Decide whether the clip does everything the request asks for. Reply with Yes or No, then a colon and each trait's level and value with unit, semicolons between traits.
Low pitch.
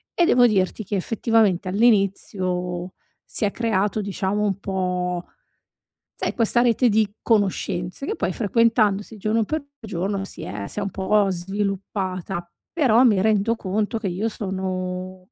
No: high, 200 Hz